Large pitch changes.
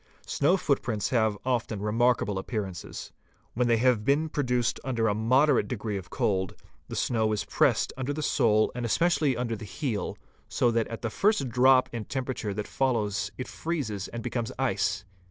No: average, 3.6 semitones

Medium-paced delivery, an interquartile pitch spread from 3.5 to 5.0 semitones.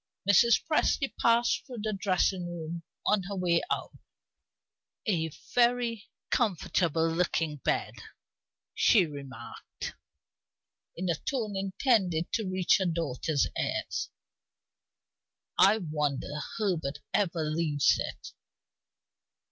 No: slow, 100 wpm; average, 4.7 semitones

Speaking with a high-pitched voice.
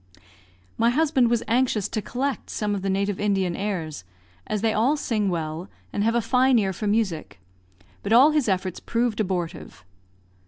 Yes: high, 210 Hz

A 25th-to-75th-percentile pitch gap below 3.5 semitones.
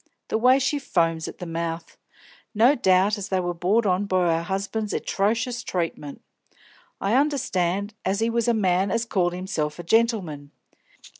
No: average, 4.4 semitones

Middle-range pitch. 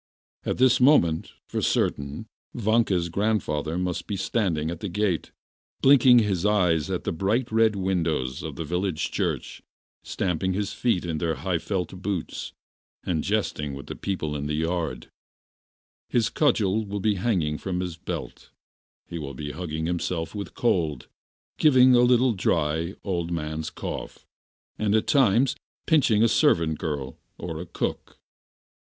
No: very low, 90 Hz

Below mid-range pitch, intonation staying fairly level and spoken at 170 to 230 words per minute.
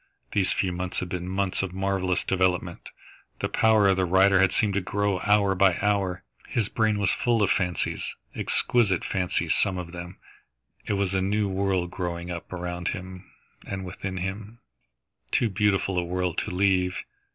Yes: very low, 95 Hz; narrow, 1.7 semitones; average, 175 wpm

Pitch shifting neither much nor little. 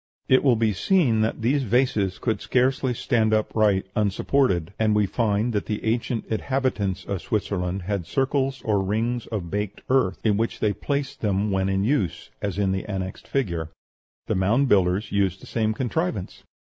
Yes: average, 4.1 semitones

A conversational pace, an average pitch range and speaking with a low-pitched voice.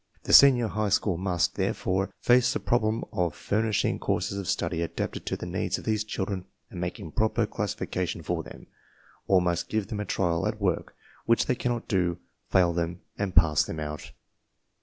Yes: average, 185 wpm; average, 3.7 semitones; very low, 95 Hz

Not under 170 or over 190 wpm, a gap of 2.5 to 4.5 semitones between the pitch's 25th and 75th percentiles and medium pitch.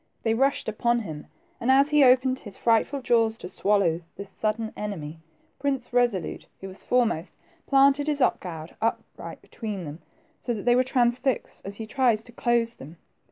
No: average, 180 wpm; average, 4.2 semitones; high, 230 Hz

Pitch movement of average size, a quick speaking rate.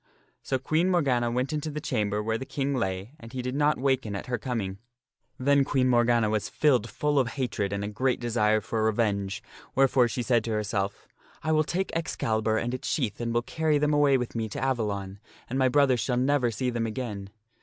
Yes: average, 3.9 semitones; fast, 215 wpm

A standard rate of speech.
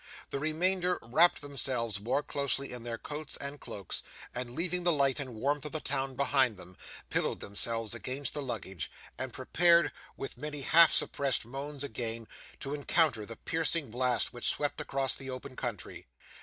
Yes: average, 170 wpm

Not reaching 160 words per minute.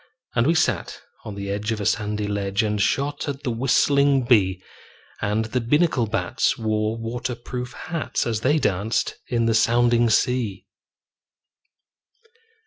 Yes: average, 145 wpm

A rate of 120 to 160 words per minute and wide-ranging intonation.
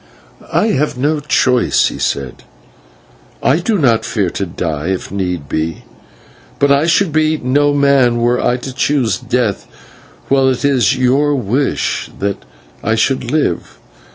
Yes: average, 150 wpm; wide, 5.9 semitones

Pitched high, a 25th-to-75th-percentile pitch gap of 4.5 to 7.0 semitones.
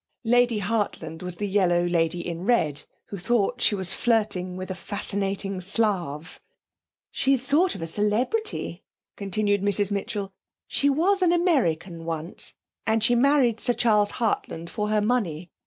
Yes: high, 205 Hz; average, 5.1 semitones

